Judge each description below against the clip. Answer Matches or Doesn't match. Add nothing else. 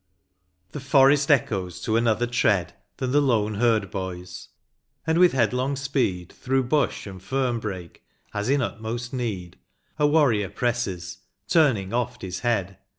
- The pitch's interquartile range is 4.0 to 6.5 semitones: Matches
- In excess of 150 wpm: Doesn't match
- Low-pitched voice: Matches